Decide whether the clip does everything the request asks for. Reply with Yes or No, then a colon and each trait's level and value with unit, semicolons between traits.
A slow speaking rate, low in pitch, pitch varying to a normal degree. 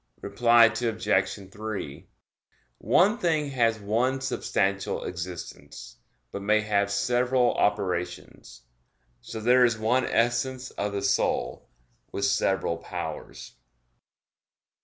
Yes: slow, 100 wpm; low, 110 Hz; average, 3.7 semitones